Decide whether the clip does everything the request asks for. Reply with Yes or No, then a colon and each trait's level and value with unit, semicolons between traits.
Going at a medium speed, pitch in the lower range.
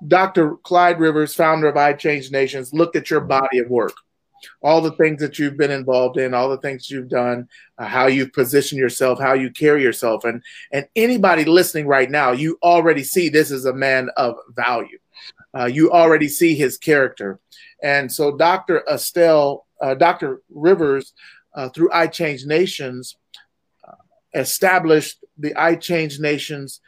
No: average, 165 wpm; medium, 150 Hz